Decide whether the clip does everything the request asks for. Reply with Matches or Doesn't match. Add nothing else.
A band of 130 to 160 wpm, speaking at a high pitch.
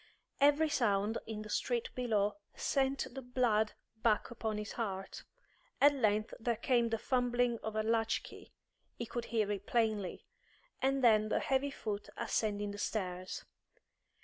Matches